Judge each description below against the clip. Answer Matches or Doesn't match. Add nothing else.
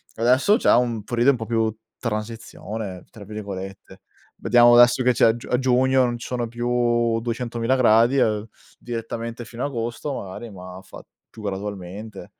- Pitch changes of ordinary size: Doesn't match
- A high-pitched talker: Doesn't match